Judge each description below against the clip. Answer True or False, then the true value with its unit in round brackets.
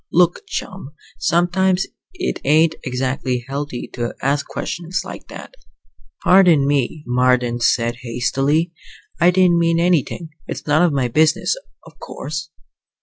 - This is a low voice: False (150 Hz)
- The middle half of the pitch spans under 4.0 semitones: False (5.3 semitones)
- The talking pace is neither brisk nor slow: False (130 wpm)